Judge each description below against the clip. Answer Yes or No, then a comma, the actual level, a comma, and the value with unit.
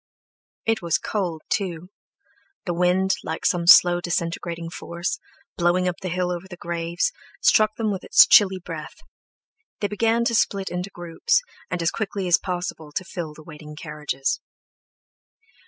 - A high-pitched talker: No, medium, 175 Hz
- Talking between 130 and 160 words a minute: Yes, average, 155 wpm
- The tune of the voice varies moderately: No, narrow, 2.3 semitones